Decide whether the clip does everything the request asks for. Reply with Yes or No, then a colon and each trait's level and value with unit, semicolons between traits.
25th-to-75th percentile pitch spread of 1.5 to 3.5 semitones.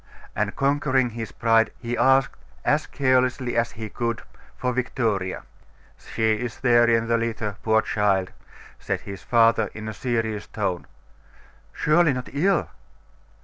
Yes: average, 2.8 semitones